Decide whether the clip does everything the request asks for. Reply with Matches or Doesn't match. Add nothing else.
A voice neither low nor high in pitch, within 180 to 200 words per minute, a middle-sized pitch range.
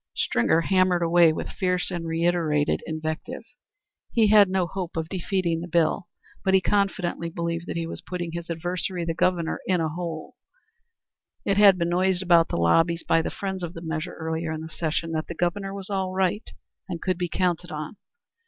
Doesn't match